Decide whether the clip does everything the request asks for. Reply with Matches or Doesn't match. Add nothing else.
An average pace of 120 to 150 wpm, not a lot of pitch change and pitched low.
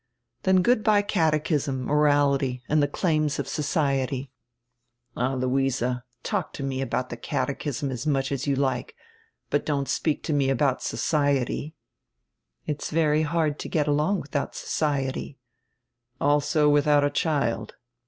Doesn't match